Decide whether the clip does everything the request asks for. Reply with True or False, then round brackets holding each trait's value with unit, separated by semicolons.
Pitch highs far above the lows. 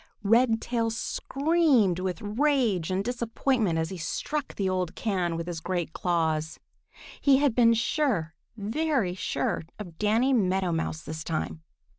True (6.1 semitones)